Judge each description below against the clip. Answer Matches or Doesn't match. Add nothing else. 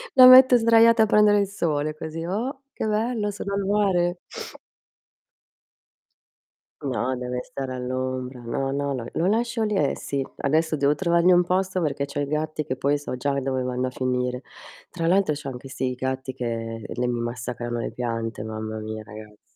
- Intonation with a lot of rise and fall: Matches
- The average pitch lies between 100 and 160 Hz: Matches